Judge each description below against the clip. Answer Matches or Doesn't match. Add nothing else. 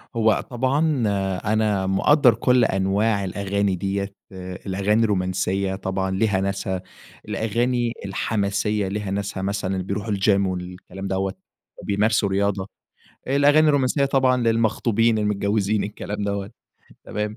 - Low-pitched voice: Matches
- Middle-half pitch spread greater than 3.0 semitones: Doesn't match